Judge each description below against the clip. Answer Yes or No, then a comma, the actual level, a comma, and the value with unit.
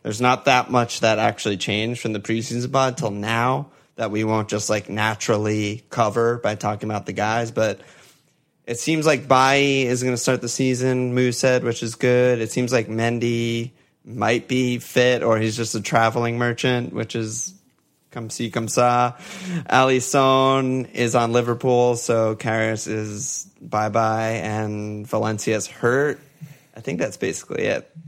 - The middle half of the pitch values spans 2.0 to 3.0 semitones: Yes, narrow, 2.5 semitones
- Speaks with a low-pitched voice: Yes, low, 120 Hz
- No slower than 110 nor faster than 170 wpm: Yes, average, 165 wpm